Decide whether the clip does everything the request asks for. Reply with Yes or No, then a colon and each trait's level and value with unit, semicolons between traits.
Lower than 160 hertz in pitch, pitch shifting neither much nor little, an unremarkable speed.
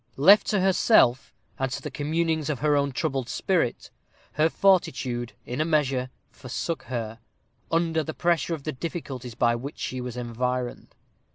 Yes: medium, 140 Hz; average, 4.5 semitones; average, 160 wpm